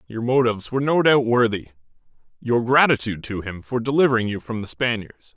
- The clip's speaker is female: No, male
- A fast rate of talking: No, average, 180 wpm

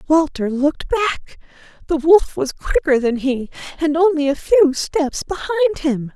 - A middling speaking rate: Yes, average, 155 wpm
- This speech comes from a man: No, female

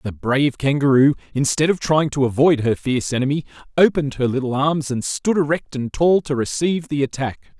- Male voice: Yes, male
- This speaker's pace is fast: No, average, 190 wpm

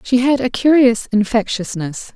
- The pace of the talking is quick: No, average, 140 wpm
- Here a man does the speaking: No, female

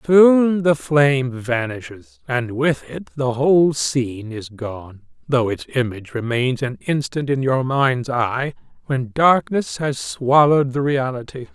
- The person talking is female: No, male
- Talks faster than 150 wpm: No, average, 145 wpm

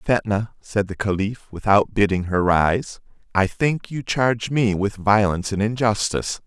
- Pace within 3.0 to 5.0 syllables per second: Yes, 4.5 syllables/s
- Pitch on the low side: Yes, low, 105 Hz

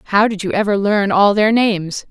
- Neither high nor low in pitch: No, high, 205 Hz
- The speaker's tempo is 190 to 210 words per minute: No, fast, 230 wpm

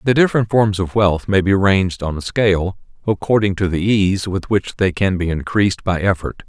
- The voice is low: Yes, very low, 95 Hz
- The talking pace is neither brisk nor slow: No, fast, 215 wpm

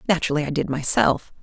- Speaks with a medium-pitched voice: Yes, medium, 155 Hz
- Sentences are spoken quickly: No, average, 170 wpm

